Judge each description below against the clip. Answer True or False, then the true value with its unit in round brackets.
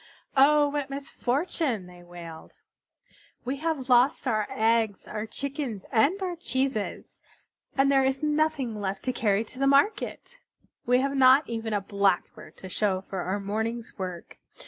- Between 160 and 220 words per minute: False (145 wpm)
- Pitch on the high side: True (245 Hz)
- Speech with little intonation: False (5.3 semitones)